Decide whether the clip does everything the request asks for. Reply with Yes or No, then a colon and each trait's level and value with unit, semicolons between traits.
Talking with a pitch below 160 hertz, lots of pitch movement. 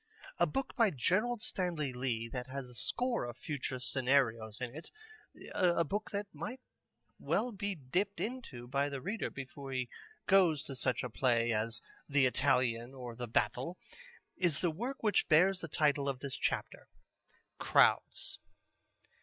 Yes: medium, 140 Hz; wide, 6.7 semitones